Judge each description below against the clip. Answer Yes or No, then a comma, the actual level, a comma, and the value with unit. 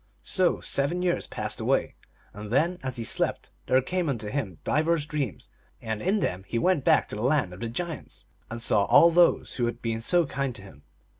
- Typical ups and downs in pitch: No, wide, 6.9 semitones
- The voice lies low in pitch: Yes, low, 130 Hz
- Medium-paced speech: No, fast, 210 wpm